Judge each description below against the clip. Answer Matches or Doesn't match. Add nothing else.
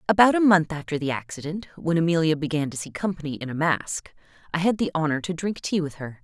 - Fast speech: Matches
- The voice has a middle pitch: Matches